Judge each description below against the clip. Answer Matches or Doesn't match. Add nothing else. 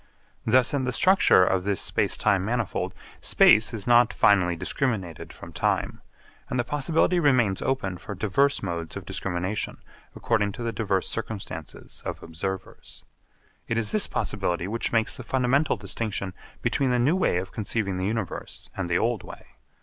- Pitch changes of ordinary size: Matches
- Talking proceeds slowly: Doesn't match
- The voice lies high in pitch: Doesn't match